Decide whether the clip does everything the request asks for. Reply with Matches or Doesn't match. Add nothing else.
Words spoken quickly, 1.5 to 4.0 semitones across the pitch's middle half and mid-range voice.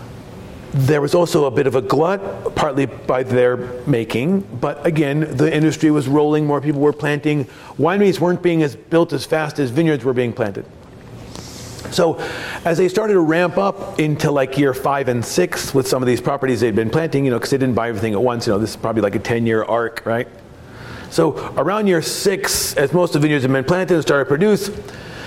Doesn't match